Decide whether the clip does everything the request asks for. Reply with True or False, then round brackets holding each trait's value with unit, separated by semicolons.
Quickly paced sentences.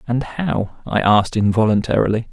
False (130 wpm)